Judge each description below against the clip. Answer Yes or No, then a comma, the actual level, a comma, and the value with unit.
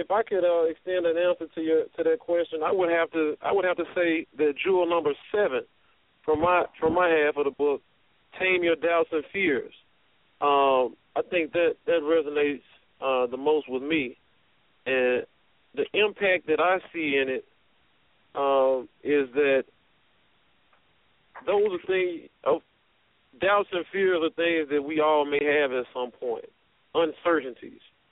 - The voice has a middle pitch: Yes, medium, 165 Hz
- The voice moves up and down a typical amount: Yes, average, 3.8 semitones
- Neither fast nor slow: Yes, average, 170 wpm